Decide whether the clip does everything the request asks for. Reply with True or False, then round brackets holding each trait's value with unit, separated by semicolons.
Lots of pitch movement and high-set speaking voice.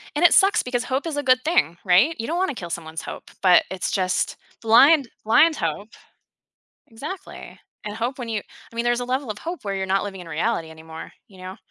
True (6.9 semitones; 225 Hz)